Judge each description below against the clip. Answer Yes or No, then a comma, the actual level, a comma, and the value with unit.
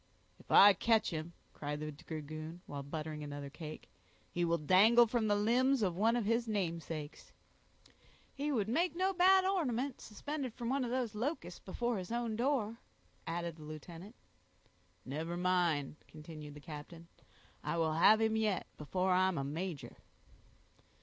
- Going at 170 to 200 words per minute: No, average, 155 wpm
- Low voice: No, medium, 185 Hz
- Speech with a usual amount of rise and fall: No, wide, 7.0 semitones